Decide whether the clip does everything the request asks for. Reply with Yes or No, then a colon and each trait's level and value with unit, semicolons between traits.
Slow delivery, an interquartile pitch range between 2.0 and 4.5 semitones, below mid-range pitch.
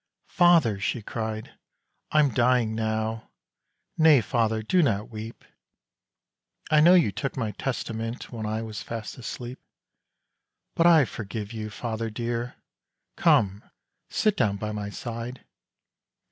Yes: slow, 125 wpm; average, 2.7 semitones; low, 115 Hz